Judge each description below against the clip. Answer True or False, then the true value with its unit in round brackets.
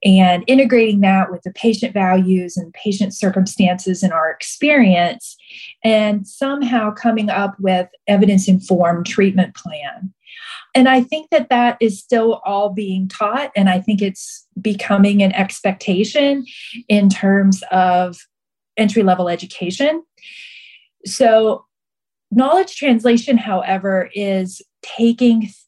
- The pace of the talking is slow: True (120 wpm)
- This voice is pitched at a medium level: False (200 Hz)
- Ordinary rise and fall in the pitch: True (3.8 semitones)